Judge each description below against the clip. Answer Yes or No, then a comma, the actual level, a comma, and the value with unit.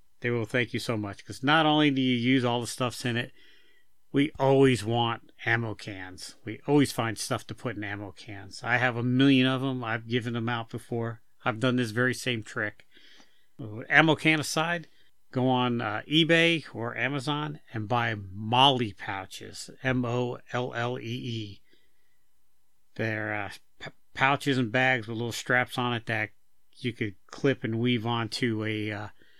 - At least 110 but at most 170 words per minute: No, average, 180 wpm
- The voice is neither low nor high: No, low, 120 Hz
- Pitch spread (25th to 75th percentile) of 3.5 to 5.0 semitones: No, average, 2.9 semitones